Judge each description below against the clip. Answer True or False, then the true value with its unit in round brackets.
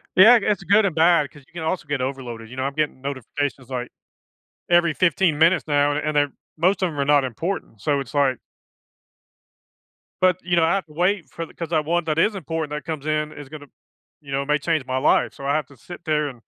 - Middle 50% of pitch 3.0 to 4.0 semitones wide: True (3.4 semitones)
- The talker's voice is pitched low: False (150 Hz)